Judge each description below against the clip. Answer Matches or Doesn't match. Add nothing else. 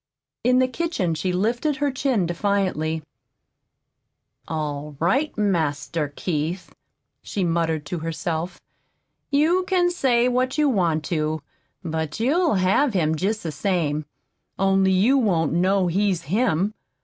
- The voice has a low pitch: Doesn't match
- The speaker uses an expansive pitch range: Matches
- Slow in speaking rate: Matches